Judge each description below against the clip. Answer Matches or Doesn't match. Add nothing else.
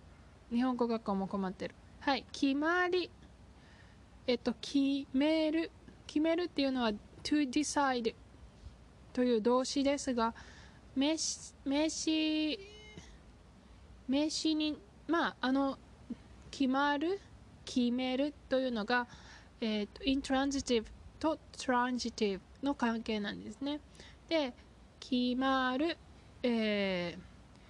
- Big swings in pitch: Doesn't match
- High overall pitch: Matches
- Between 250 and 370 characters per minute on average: Doesn't match